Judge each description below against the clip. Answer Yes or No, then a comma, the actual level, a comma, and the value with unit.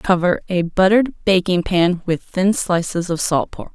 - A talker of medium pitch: Yes, medium, 180 Hz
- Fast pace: No, average, 175 wpm